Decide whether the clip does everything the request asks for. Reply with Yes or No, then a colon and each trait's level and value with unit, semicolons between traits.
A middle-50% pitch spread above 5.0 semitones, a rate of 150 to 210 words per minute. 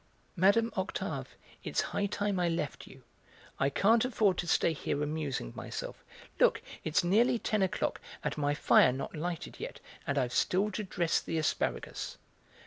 Yes: wide, 5.5 semitones; average, 160 wpm